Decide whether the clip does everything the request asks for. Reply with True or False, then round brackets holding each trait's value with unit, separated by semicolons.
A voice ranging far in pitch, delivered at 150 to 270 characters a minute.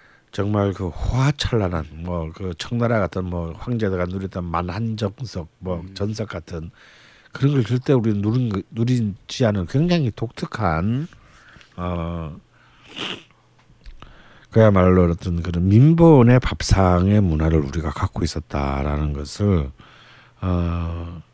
False (4.9 semitones; 230 characters per minute)